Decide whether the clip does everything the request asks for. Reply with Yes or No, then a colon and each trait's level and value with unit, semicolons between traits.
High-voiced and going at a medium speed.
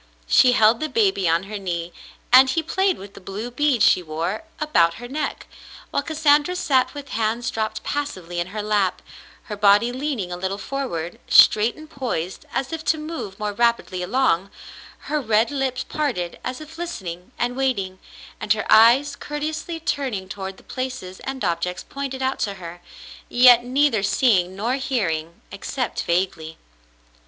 Yes: high, 235 Hz; average, 165 wpm